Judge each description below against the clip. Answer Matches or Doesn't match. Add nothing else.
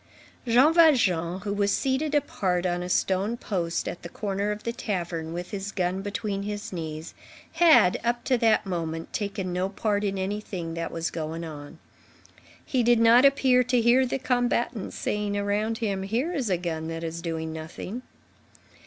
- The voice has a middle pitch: Doesn't match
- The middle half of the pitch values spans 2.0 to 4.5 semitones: Doesn't match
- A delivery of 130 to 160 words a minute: Doesn't match